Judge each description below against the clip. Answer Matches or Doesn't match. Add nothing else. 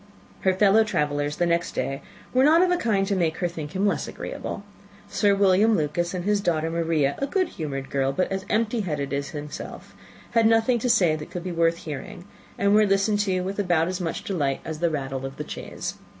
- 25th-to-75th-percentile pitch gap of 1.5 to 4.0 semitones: Doesn't match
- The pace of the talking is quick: Matches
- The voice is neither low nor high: Matches